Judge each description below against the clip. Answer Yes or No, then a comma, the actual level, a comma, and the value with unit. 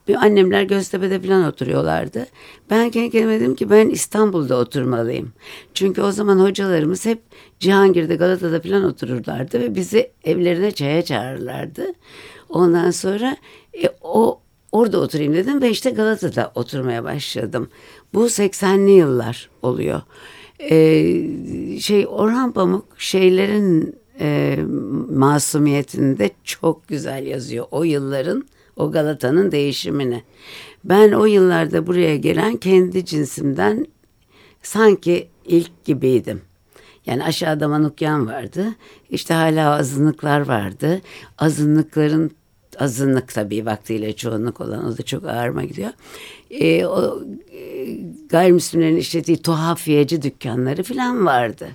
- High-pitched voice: No, medium, 165 Hz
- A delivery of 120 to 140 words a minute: No, average, 110 wpm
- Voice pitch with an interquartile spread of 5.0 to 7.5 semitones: Yes, wide, 5.6 semitones